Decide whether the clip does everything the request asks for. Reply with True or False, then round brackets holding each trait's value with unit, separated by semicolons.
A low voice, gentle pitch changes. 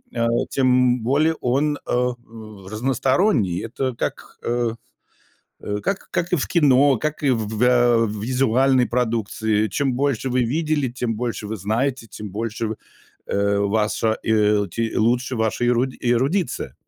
False (120 Hz; 3.2 semitones)